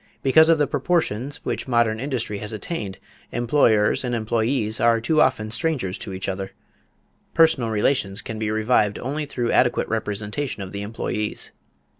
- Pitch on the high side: No, low, 115 Hz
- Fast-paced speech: No, average, 155 wpm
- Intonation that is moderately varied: Yes, average, 4.3 semitones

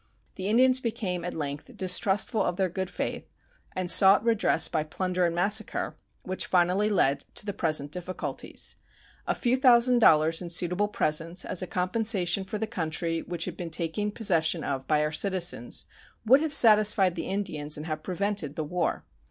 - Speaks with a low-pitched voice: No, medium, 185 Hz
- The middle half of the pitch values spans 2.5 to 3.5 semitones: No, average, 4.1 semitones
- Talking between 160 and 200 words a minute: Yes, average, 175 wpm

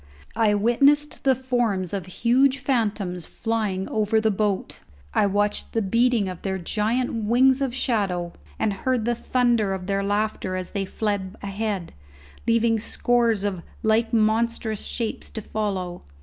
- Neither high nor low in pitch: No, high, 220 Hz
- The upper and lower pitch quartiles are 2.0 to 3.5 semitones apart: Yes, average, 3.1 semitones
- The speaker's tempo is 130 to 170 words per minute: Yes, average, 150 wpm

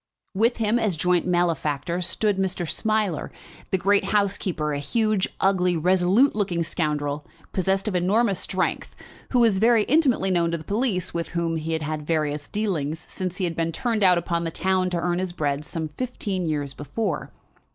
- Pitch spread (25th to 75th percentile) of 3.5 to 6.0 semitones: Yes, average, 3.8 semitones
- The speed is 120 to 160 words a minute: No, average, 180 wpm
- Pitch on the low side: No, medium, 180 Hz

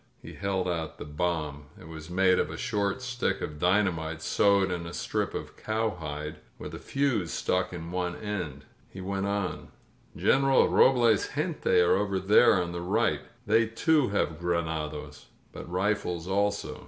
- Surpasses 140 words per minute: Yes, average, 165 wpm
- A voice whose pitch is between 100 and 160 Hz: No, very low, 90 Hz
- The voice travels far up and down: No, average, 4.1 semitones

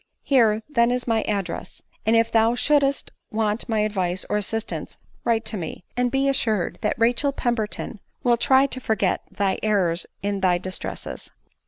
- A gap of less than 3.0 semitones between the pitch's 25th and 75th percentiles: No, average, 3.3 semitones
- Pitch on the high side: Yes, high, 225 Hz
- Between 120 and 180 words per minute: Yes, average, 165 wpm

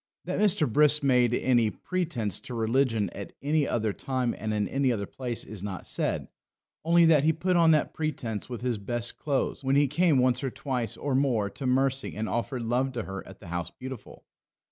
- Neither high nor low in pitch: No, low, 130 Hz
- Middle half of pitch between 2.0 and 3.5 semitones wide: No, average, 4.1 semitones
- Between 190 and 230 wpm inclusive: Yes, fast, 205 wpm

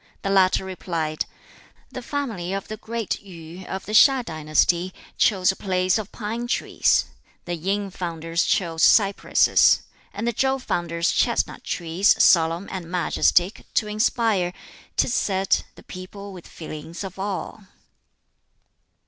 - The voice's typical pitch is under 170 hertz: No, high, 190 Hz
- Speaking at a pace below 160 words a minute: Yes, slow, 135 wpm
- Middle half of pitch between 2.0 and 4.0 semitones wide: Yes, average, 3.4 semitones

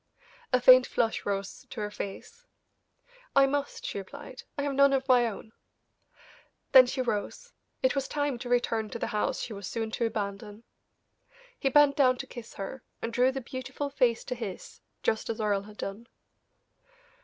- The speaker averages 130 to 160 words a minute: No, average, 180 wpm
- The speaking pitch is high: Yes, high, 245 Hz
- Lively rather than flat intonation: No, average, 4.0 semitones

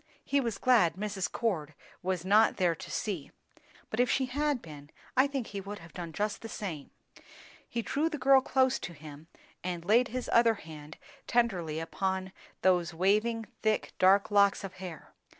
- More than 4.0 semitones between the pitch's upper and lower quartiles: Yes, wide, 5.5 semitones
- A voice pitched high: Yes, high, 200 Hz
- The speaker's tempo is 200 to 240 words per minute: No, average, 175 wpm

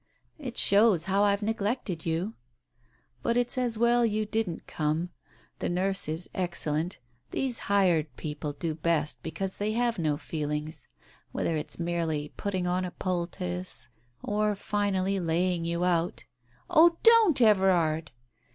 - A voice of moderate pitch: Yes, medium, 180 Hz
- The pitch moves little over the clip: No, average, 4.5 semitones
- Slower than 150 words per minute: Yes, average, 140 wpm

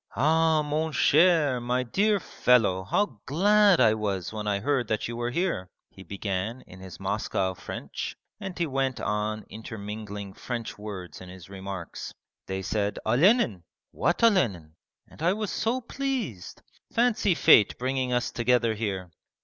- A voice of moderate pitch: No, low, 120 Hz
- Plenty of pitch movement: Yes, wide, 8.4 semitones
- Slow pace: No, average, 150 wpm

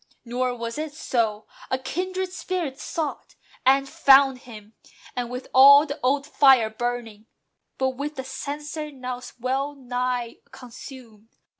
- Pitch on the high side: Yes, very high, 260 Hz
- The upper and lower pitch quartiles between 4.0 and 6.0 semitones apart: No, average, 2.8 semitones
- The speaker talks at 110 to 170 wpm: Yes, slow, 135 wpm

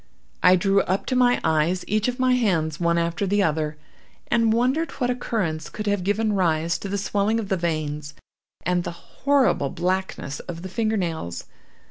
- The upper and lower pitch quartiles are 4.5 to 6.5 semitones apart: Yes, average, 4.9 semitones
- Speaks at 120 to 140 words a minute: No, average, 175 wpm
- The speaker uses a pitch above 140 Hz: Yes, high, 190 Hz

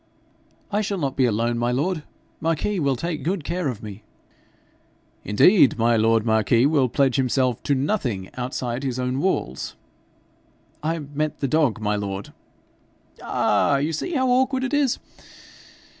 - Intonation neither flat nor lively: No, wide, 6.0 semitones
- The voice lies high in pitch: No, low, 135 Hz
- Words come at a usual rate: Yes, average, 150 wpm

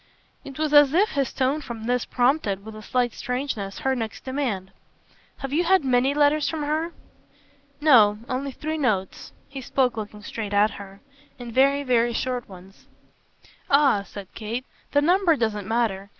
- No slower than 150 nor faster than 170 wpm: Yes, average, 165 wpm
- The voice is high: Yes, very high, 250 Hz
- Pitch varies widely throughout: No, average, 4.9 semitones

